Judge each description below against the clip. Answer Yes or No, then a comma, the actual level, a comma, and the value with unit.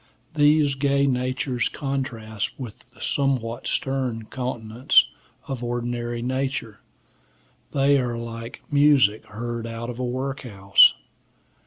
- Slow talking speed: Yes, slow, 110 wpm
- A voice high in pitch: No, low, 125 Hz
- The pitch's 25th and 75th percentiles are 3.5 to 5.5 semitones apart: No, average, 2.8 semitones